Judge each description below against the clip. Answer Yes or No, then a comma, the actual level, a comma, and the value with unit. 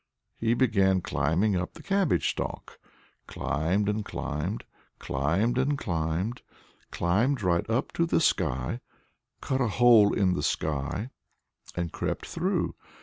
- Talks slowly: Yes, slow, 130 wpm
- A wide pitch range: Yes, wide, 6.5 semitones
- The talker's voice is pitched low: Yes, low, 100 Hz